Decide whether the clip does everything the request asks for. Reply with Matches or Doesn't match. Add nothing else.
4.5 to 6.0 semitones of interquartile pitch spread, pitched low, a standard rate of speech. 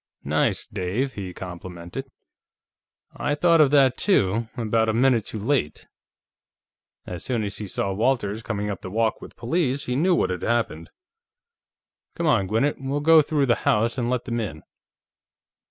Matches